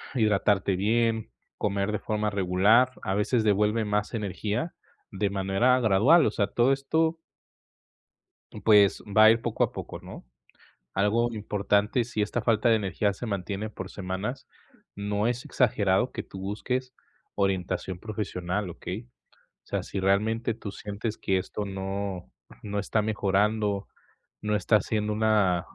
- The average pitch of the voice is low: Yes, low, 105 Hz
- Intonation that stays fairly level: Yes, narrow, 2.3 semitones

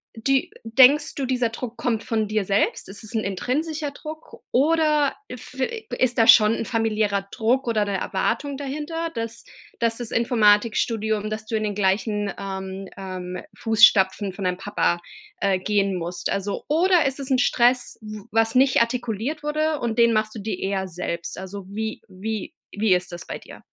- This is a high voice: Yes, high, 220 Hz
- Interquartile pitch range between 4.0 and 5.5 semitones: Yes, average, 4.4 semitones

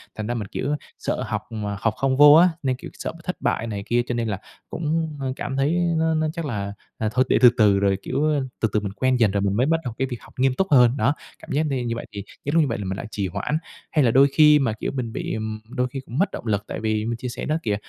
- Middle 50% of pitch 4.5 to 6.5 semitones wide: Yes, average, 5.1 semitones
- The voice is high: No, low, 125 Hz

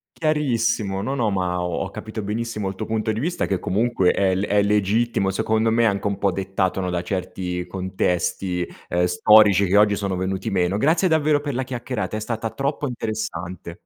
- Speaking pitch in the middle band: No, low, 105 Hz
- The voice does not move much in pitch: No, average, 3.5 semitones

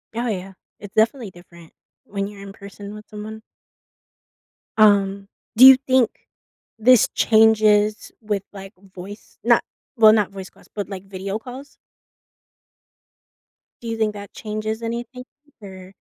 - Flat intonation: Yes, narrow, 2.1 semitones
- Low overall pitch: No, high, 210 Hz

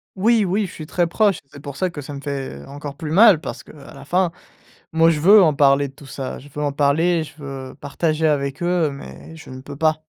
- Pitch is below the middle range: No, medium, 150 Hz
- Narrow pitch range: No, average, 3.5 semitones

